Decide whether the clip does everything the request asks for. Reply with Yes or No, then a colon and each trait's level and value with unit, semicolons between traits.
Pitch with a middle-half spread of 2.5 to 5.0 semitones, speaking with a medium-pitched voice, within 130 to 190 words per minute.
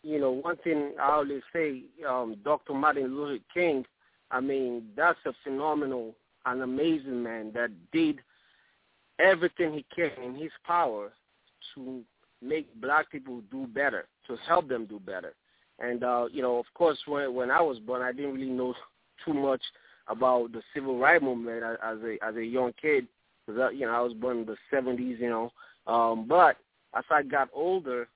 No: average, 3.6 semitones; low, 130 Hz; average, 180 wpm